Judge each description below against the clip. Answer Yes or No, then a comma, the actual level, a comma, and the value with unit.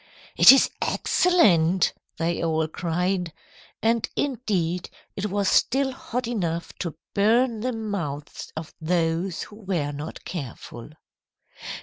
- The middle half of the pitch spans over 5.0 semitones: Yes, wide, 5.4 semitones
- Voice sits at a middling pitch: Yes, medium, 180 Hz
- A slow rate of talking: Yes, slow, 115 wpm